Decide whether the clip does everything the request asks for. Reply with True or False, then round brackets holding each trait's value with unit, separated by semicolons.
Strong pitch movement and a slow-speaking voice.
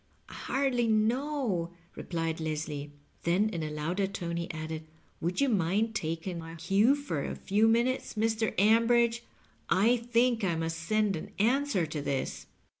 False (6.0 semitones; 155 wpm)